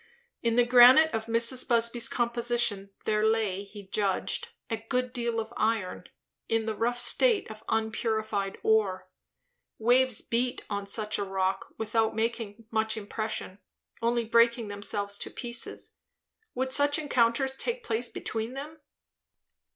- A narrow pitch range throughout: Yes, narrow, 2.2 semitones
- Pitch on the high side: Yes, high, 225 Hz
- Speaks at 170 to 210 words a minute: No, slow, 135 wpm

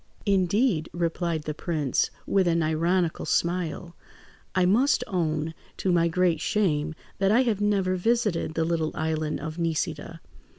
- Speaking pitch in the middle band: Yes, medium, 170 Hz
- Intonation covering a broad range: No, average, 3.1 semitones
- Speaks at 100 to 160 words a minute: Yes, average, 140 wpm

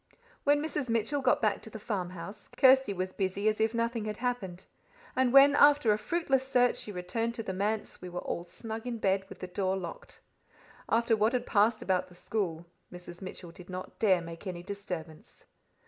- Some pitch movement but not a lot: Yes, average, 4.4 semitones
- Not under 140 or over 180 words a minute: No, average, 195 wpm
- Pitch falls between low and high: No, high, 210 Hz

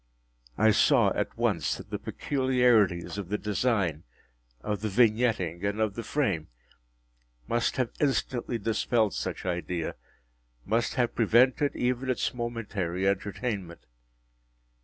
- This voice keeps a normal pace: No, slow, 115 wpm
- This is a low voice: Yes, low, 110 Hz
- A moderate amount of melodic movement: Yes, average, 4.5 semitones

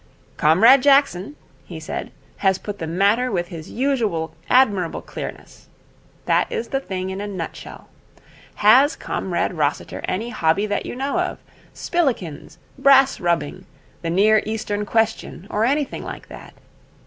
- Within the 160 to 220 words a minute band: No, average, 140 wpm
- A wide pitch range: Yes, wide, 6.3 semitones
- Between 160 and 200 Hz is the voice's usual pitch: No, high, 210 Hz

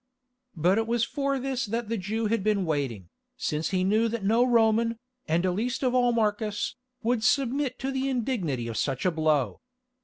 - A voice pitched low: No, high, 220 Hz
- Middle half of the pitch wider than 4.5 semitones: Yes, average, 5.1 semitones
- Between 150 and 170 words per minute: No, average, 185 wpm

